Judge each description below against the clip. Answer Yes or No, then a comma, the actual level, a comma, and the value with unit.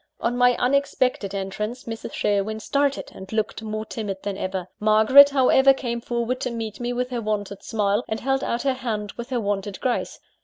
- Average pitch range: Yes, average, 3.4 semitones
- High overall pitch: Yes, high, 225 Hz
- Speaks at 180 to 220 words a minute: Yes, average, 190 wpm